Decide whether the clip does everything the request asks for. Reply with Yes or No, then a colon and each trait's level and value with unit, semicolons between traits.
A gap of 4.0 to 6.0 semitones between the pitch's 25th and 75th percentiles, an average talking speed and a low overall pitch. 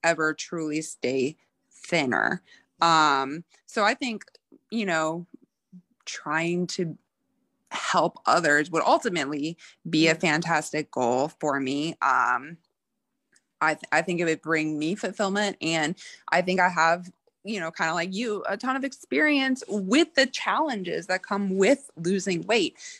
No: wide, 5.6 semitones; average, 145 wpm; medium, 175 Hz